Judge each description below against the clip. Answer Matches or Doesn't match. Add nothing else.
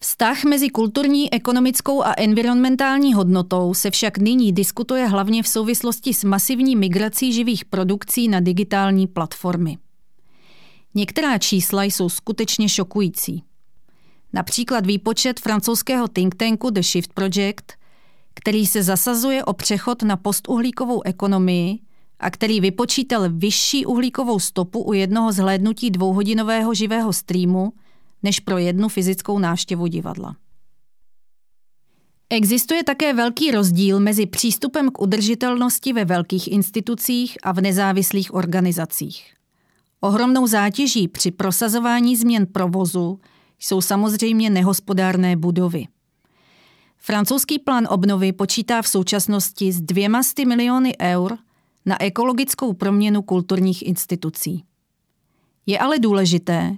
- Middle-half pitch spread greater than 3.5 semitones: Matches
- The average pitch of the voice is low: Doesn't match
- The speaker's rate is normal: Doesn't match